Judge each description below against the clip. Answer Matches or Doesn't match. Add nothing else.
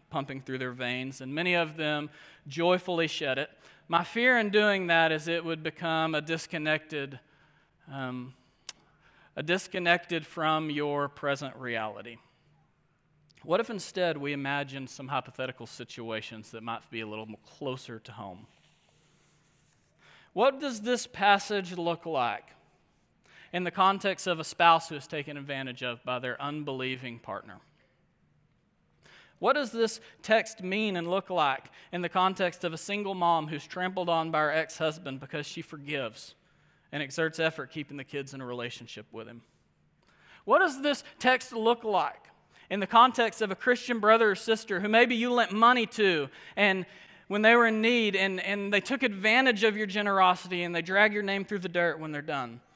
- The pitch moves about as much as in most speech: Doesn't match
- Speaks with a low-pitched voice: Doesn't match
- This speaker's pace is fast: Doesn't match